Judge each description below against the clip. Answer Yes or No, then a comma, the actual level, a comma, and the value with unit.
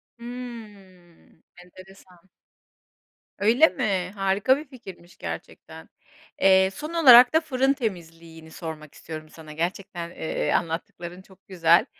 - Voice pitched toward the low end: No, high, 190 Hz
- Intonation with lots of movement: Yes, wide, 5.8 semitones